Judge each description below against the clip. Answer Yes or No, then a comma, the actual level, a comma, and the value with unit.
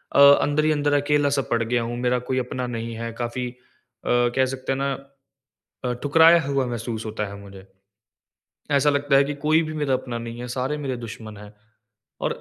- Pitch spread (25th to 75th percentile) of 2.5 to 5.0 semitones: Yes, average, 3.5 semitones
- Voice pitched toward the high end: No, low, 130 Hz